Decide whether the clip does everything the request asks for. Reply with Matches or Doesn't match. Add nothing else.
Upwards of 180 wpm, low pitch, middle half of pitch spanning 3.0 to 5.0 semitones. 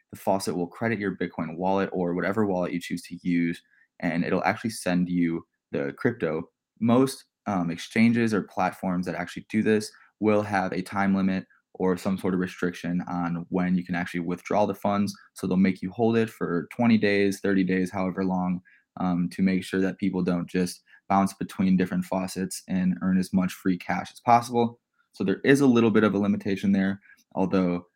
Doesn't match